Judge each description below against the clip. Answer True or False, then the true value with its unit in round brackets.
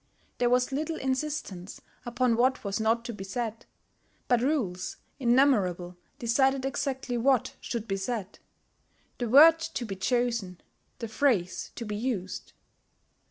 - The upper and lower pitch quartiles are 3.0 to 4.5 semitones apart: True (4.2 semitones)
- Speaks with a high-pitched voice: True (240 Hz)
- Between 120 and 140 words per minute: True (135 wpm)